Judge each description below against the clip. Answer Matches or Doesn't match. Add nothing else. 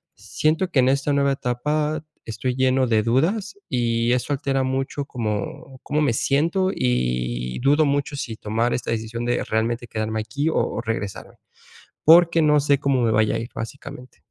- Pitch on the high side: Doesn't match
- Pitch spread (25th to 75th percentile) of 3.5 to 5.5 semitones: Matches